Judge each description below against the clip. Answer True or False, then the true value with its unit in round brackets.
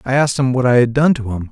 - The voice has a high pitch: False (125 Hz)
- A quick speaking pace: True (355 wpm)